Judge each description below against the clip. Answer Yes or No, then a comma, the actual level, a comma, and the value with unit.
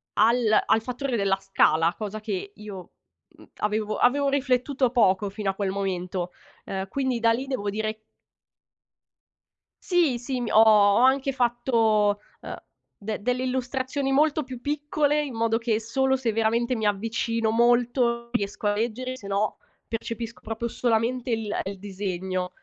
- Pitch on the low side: No, high, 230 Hz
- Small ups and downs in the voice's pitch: No, average, 3.6 semitones